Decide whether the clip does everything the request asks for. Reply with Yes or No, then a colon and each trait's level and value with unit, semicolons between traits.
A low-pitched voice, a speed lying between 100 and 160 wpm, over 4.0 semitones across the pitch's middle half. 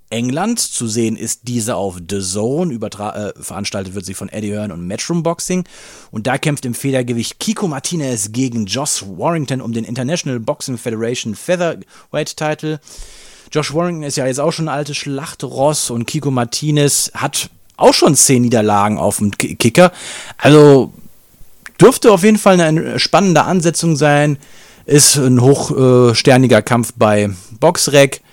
Yes: low, 130 Hz; average, 155 wpm; average, 5.1 semitones